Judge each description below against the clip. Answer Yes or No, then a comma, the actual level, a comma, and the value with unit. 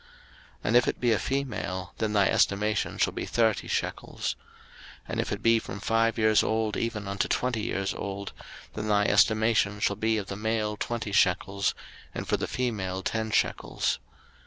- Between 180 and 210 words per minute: Yes, average, 185 wpm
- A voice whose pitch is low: Yes, low, 105 Hz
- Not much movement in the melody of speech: Yes, narrow, 2.1 semitones